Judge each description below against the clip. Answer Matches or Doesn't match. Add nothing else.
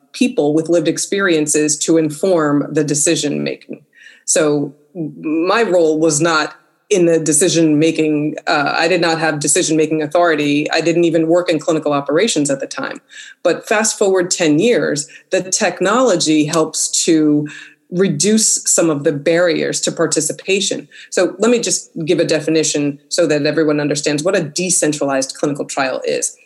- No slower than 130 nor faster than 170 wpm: Matches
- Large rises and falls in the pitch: Doesn't match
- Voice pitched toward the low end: Doesn't match